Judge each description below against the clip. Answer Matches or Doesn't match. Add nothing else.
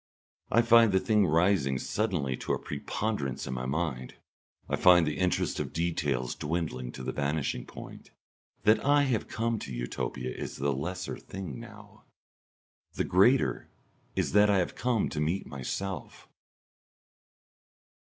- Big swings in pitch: Matches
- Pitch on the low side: Matches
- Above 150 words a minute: Doesn't match